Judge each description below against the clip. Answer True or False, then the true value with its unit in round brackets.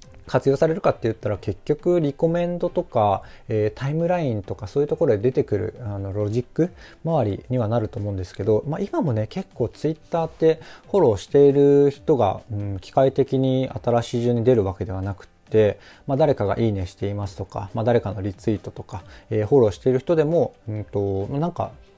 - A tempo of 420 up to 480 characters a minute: True (430 characters per minute)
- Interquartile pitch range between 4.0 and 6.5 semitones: True (5.6 semitones)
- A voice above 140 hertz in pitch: False (120 Hz)